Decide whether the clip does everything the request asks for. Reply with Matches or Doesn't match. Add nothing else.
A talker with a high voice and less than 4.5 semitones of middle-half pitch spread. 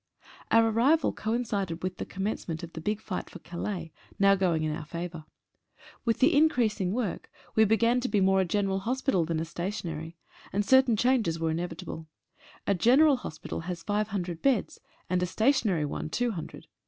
Doesn't match